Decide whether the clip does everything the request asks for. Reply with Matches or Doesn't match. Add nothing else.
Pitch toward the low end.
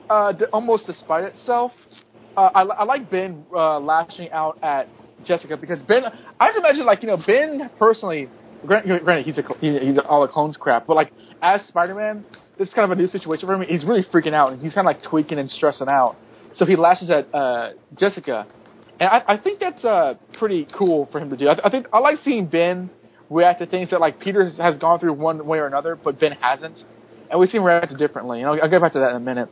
Doesn't match